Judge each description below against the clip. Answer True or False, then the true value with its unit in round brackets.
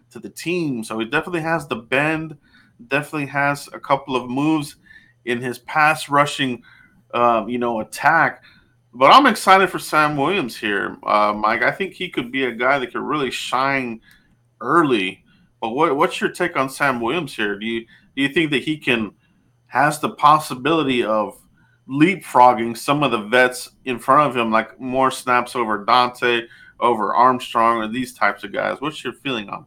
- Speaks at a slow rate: False (180 wpm)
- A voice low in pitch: True (130 Hz)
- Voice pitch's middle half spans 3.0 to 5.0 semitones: True (4.0 semitones)